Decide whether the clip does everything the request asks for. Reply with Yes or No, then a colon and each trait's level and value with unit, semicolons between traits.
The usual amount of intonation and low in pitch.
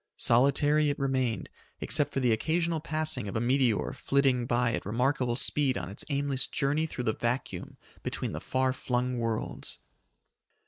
Yes: average, 3.1 semitones; low, 130 Hz